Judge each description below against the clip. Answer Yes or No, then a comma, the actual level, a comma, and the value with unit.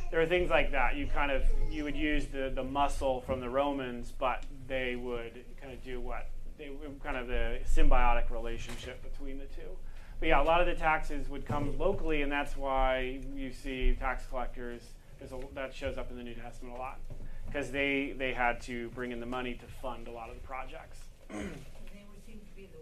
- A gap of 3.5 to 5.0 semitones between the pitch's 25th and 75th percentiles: No, average, 2.7 semitones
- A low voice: Yes, low, 130 Hz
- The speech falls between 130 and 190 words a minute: No, average, 200 wpm